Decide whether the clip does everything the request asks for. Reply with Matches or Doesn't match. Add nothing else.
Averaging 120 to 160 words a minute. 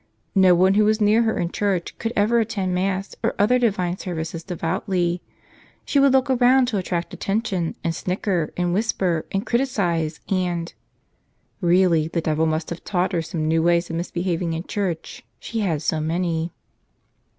Doesn't match